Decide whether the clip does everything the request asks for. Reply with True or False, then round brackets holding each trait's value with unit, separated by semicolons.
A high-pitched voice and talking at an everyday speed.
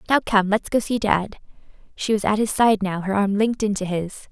False (205 Hz; 235 wpm)